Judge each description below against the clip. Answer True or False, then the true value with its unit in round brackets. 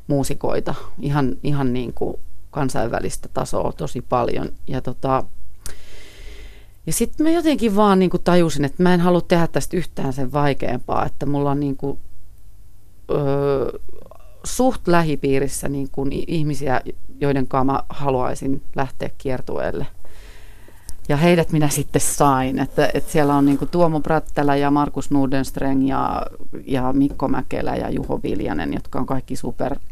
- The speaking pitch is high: False (140 Hz)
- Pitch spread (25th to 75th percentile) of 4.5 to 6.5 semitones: False (2.7 semitones)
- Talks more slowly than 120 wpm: False (140 wpm)